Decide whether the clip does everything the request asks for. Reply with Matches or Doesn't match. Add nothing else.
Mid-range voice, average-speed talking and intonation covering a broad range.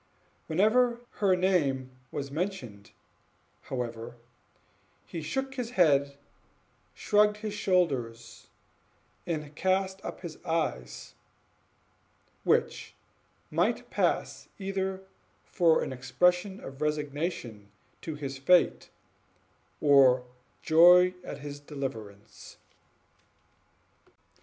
Doesn't match